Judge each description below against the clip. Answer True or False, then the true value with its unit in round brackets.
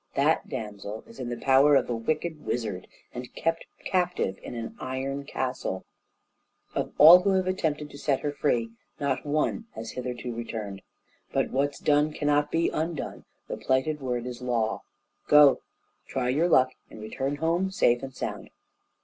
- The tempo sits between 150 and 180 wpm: True (165 wpm)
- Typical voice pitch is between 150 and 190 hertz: False (135 Hz)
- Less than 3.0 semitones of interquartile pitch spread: False (3.9 semitones)